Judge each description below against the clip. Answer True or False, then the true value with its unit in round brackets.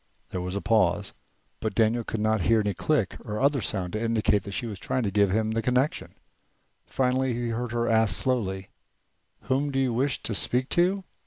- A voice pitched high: False (115 Hz)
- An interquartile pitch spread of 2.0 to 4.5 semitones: True (3.6 semitones)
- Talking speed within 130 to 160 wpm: False (200 wpm)